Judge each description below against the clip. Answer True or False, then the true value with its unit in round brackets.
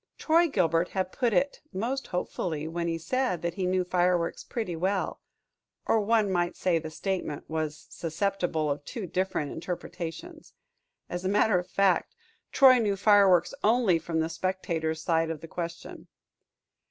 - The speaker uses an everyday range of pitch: True (3.5 semitones)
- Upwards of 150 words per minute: True (160 wpm)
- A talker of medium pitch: True (180 Hz)